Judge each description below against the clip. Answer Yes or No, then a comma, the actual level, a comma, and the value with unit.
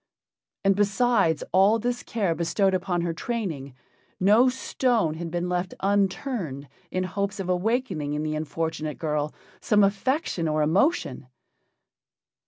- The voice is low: No, medium, 185 Hz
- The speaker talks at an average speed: No, slow, 130 wpm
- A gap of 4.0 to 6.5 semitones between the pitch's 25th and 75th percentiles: Yes, average, 4.7 semitones